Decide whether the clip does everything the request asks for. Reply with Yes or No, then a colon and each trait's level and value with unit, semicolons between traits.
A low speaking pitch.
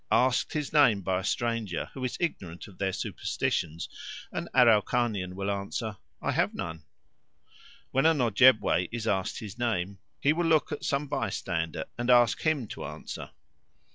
Yes: low, 115 Hz